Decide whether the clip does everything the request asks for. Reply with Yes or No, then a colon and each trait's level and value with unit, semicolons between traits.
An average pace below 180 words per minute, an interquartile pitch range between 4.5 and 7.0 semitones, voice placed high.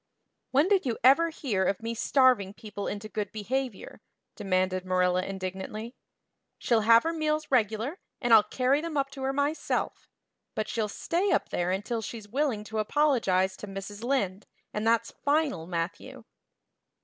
Yes: average, 160 wpm; wide, 5.6 semitones; high, 225 Hz